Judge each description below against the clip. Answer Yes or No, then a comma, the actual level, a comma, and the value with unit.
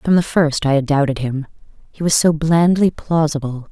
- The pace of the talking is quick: No, average, 195 wpm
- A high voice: No, medium, 150 Hz